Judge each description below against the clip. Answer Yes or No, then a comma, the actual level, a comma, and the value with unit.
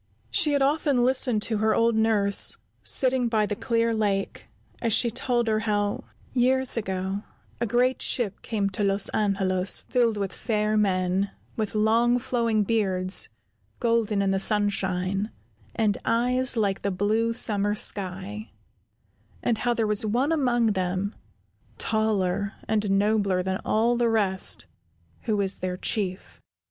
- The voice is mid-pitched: No, high, 215 Hz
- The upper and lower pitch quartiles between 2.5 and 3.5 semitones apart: Yes, average, 2.9 semitones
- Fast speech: No, average, 145 wpm